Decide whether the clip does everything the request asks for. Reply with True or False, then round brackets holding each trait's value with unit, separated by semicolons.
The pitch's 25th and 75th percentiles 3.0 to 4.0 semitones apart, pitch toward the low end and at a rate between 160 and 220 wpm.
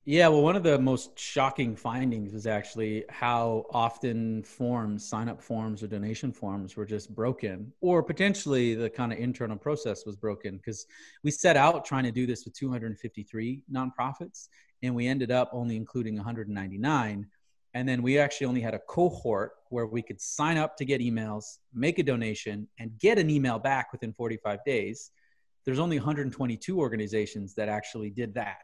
True (3.7 semitones; 120 Hz; 175 wpm)